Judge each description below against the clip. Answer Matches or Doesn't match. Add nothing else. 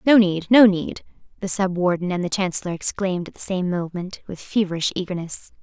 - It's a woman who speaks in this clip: Matches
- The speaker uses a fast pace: Doesn't match